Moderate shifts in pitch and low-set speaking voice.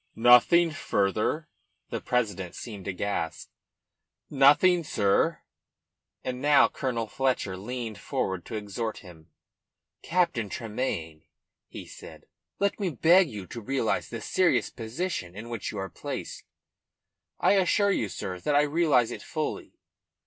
No: wide, 6.8 semitones; low, 115 Hz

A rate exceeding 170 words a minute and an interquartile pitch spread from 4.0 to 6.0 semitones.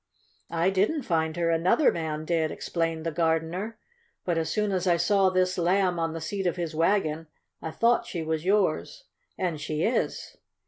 No: average, 180 wpm; average, 2.9 semitones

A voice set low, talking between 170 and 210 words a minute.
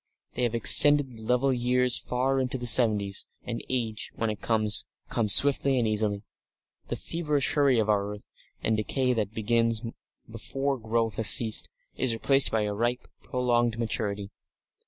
No: low, 115 Hz; average, 160 wpm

